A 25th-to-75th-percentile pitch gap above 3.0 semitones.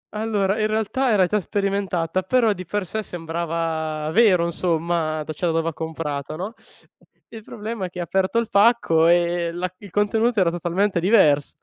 Yes: average, 4.1 semitones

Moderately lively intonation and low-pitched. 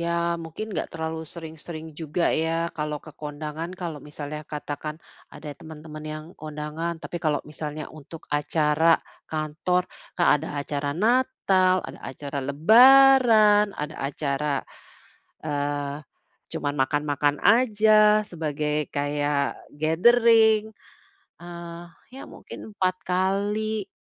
No: average, 4.1 semitones; medium, 160 Hz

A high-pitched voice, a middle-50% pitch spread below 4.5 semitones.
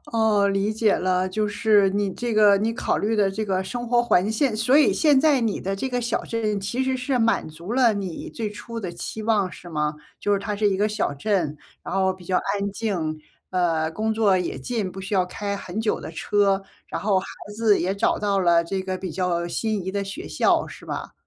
Yes: high, 200 Hz; average, 2.9 semitones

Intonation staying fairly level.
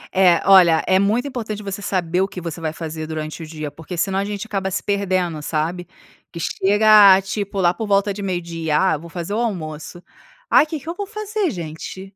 No: average, 3.6 semitones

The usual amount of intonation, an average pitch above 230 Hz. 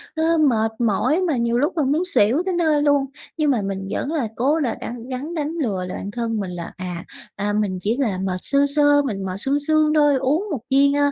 No: wide, 6.1 semitones; very high, 270 Hz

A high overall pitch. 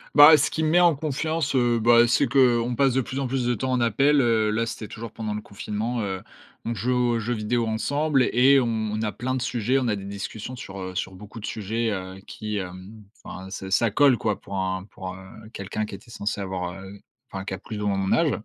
No: low, 110 Hz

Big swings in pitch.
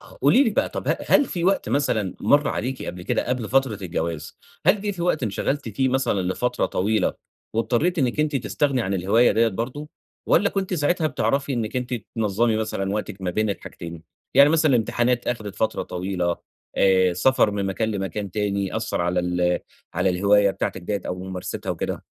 Yes: wide, 6.0 semitones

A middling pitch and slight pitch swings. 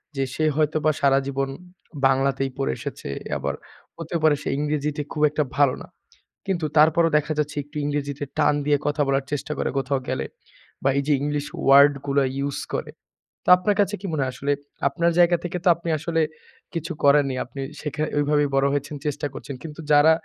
Yes: medium, 145 Hz; narrow, 2.1 semitones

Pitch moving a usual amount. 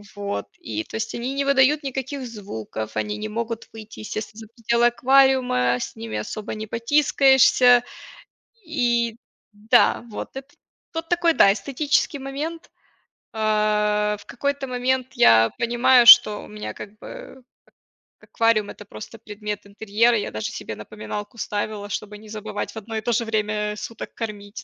Yes: average, 3.6 semitones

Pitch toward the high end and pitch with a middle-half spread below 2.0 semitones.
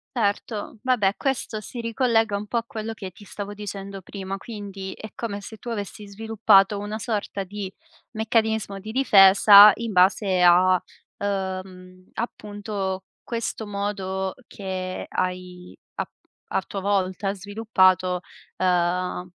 No: high, 200 Hz; narrow, 2.4 semitones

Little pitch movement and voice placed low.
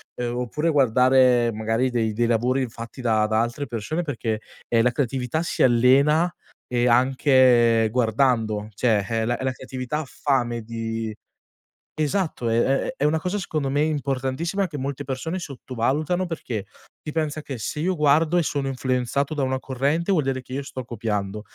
No: average, 4.0 semitones; low, 130 Hz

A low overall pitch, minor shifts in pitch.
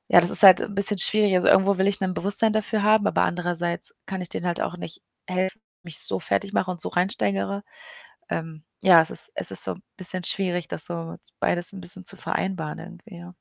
No: medium, 185 Hz; narrow, 2.3 semitones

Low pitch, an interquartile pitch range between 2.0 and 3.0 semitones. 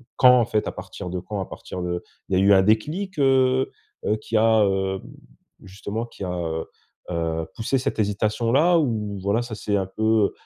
No: low, 105 Hz; average, 3.8 semitones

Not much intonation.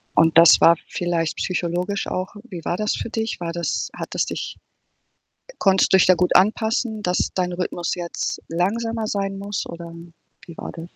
No: average, 3.0 semitones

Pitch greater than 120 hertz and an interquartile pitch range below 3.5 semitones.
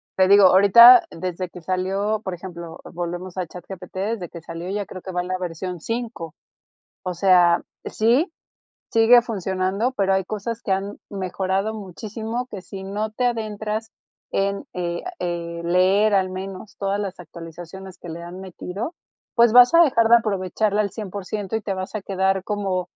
Yes: high, 190 Hz; average, 2.9 semitones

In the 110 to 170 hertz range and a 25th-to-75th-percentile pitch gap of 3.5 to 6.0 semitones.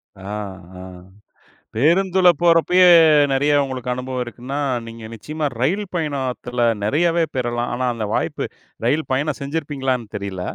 Yes: low, 135 Hz; average, 4.7 semitones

